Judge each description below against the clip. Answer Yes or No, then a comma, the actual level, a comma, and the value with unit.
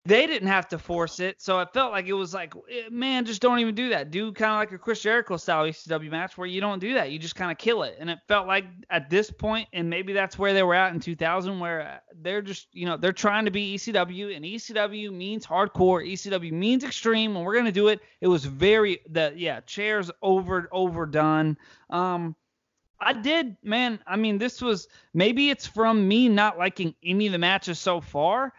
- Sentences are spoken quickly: Yes, fast, 225 wpm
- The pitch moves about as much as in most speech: Yes, average, 3.7 semitones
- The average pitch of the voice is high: Yes, high, 195 Hz